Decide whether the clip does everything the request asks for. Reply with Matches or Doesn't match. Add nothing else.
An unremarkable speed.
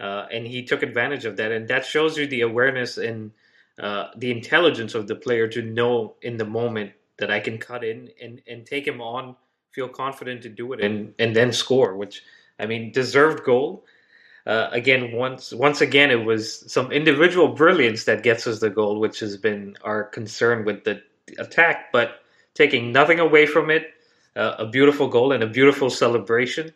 Matches